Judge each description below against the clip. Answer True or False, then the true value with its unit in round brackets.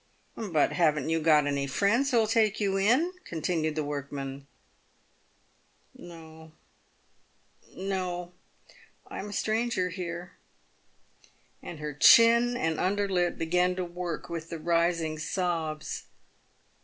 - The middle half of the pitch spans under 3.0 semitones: False (3.9 semitones)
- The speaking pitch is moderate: True (175 Hz)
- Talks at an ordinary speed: False (130 wpm)